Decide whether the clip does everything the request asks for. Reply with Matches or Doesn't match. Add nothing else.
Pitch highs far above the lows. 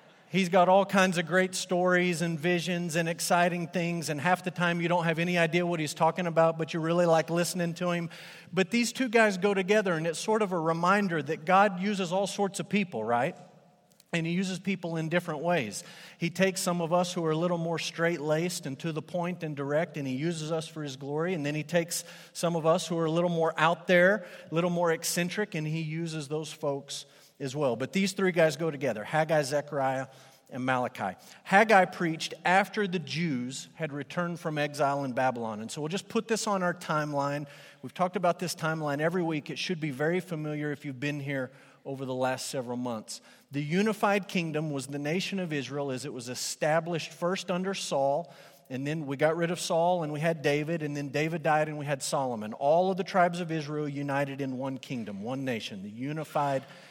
Doesn't match